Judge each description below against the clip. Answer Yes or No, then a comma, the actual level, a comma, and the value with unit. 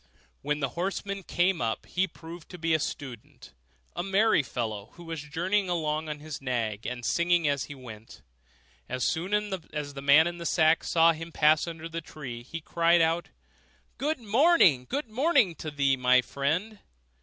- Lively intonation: No, average, 4.1 semitones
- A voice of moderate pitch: Yes, medium, 160 Hz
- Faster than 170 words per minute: Yes, average, 180 wpm